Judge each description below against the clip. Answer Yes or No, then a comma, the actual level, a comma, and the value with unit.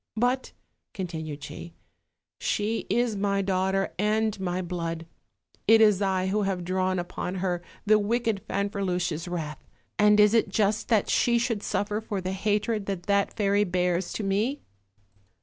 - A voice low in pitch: No, high, 195 Hz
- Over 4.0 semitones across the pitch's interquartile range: No, narrow, 2.6 semitones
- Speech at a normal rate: Yes, average, 150 wpm